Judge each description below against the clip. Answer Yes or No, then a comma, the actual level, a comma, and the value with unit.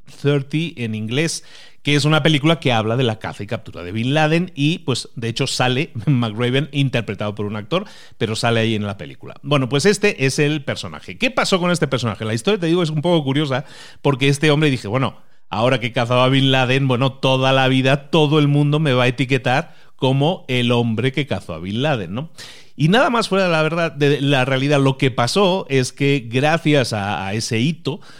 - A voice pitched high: No, low, 135 Hz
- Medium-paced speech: No, fast, 220 wpm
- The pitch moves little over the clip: No, average, 4.0 semitones